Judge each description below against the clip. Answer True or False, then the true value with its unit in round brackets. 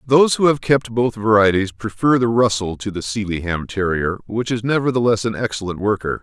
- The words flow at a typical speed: True (185 wpm)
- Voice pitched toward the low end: True (110 Hz)